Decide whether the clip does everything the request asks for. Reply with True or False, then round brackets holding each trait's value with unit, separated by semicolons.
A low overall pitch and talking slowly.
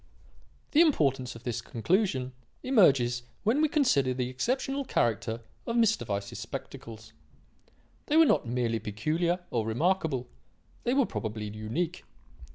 True (130 Hz; 130 wpm)